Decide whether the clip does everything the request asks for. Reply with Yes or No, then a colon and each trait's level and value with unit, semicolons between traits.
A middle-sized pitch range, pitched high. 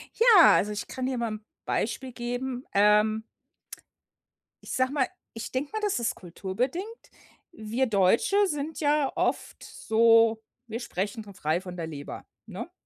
Yes: average, 4.1 semitones; high, 230 Hz